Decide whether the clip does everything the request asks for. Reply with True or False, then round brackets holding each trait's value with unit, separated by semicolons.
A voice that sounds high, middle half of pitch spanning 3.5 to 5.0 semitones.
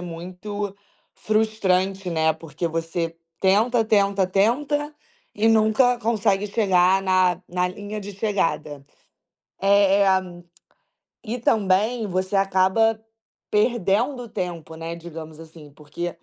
True (195 Hz; 3.8 semitones)